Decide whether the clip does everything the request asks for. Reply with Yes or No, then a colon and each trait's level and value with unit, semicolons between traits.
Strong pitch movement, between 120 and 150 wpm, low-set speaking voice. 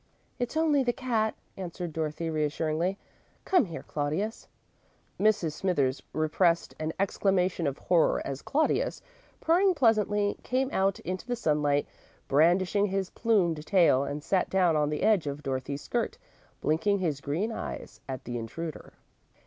No: wide, 5.8 semitones; average, 140 wpm; medium, 175 Hz